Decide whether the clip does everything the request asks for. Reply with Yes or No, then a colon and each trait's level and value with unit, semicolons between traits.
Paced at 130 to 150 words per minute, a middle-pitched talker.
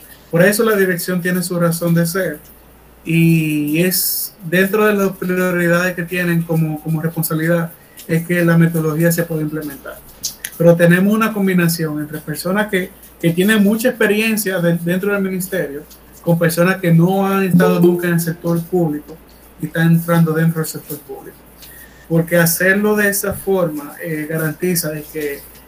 No: average, 160 wpm; medium, 170 Hz